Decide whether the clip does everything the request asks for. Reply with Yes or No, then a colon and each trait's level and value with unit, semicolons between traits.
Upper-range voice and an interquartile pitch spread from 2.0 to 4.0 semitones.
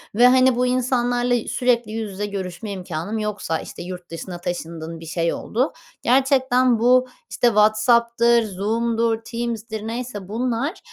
Yes: high, 230 Hz; average, 3.6 semitones